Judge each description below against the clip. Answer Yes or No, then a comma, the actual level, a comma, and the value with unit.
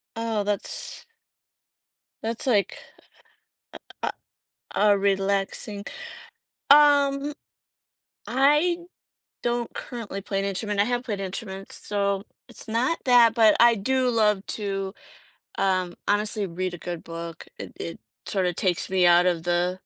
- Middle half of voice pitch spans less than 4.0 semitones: Yes, average, 3.6 semitones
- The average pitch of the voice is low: No, high, 205 Hz